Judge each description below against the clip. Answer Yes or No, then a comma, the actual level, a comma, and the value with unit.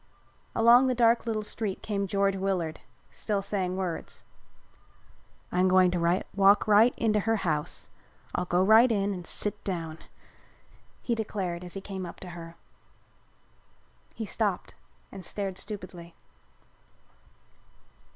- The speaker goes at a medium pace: No, slow, 130 wpm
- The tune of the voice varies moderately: Yes, average, 3.0 semitones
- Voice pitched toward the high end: Yes, high, 195 Hz